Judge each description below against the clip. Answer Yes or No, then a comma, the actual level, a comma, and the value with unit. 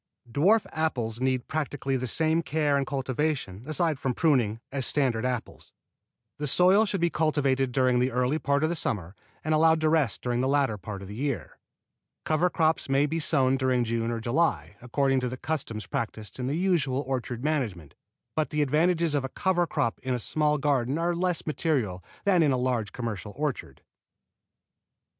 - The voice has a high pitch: No, low, 135 Hz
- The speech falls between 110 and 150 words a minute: No, average, 185 wpm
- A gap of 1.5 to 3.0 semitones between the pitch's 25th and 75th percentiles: No, average, 4.2 semitones